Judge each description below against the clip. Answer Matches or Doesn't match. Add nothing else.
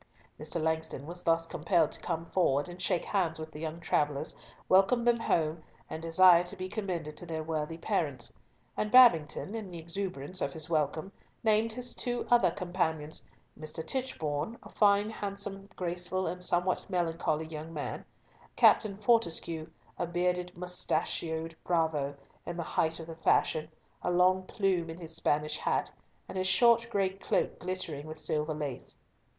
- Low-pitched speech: Doesn't match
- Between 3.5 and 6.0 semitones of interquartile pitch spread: Doesn't match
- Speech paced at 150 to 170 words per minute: Matches